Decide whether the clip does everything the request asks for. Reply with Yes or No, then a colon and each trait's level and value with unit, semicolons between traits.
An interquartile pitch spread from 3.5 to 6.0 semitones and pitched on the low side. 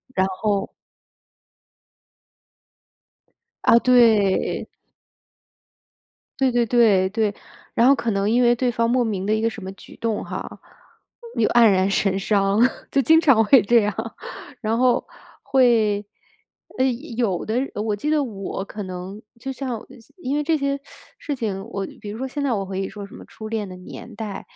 No: average, 3.8 semitones; high, 220 Hz